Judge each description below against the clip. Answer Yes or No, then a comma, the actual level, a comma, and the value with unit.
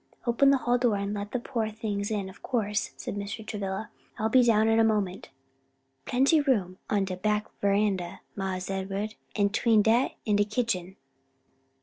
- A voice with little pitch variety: Yes, narrow, 2.3 semitones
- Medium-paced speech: Yes, average, 185 wpm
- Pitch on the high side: Yes, high, 210 Hz